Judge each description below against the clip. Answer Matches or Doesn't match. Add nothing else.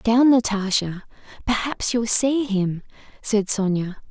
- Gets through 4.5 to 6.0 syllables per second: Doesn't match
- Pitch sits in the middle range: Doesn't match